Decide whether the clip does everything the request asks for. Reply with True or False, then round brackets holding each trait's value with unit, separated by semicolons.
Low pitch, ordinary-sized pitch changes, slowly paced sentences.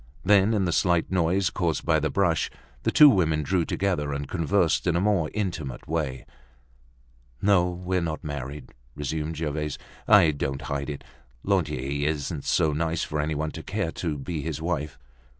False (80 Hz; 3.5 semitones; 170 wpm)